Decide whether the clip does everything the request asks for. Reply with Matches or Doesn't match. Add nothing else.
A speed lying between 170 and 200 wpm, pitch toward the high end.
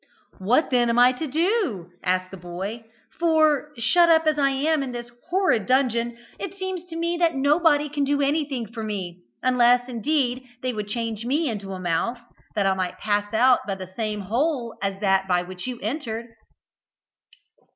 Matches